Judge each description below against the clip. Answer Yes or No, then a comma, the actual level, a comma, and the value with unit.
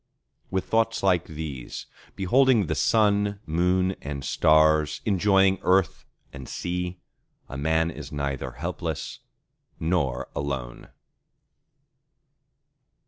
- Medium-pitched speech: No, very low, 85 Hz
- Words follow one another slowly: Yes, slow, 95 wpm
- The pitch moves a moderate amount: Yes, average, 4.9 semitones